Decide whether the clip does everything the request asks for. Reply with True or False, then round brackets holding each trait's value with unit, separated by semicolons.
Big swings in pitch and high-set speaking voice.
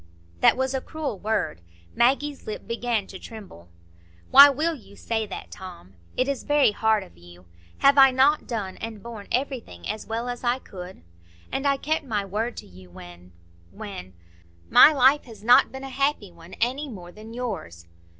True (7.2 semitones; 220 Hz)